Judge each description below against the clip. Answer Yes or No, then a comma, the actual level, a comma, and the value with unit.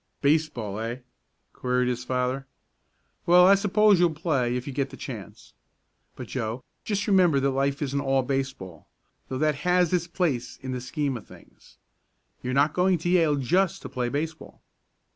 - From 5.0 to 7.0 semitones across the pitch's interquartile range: Yes, average, 5.3 semitones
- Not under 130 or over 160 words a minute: No, average, 170 wpm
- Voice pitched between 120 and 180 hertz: Yes, medium, 140 Hz